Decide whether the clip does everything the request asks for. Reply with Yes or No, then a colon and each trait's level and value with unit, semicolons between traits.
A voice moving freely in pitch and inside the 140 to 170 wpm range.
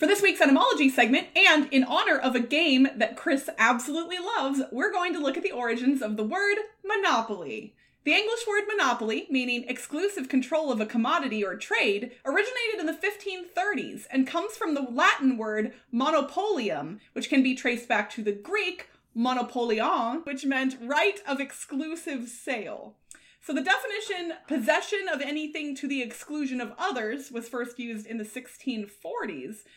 Yes: wide, 6.0 semitones; average, 165 wpm